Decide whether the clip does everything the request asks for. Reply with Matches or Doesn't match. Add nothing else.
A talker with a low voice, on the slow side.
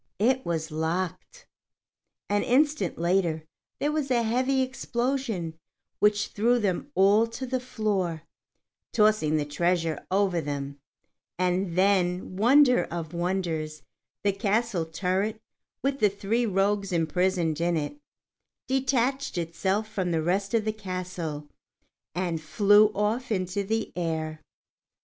Doesn't match